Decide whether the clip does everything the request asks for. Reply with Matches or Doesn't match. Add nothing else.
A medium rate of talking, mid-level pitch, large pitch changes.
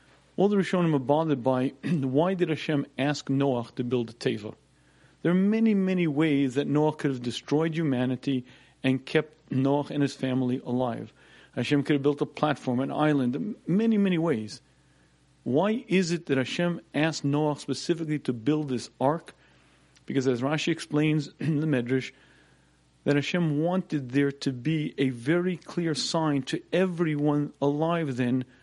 Doesn't match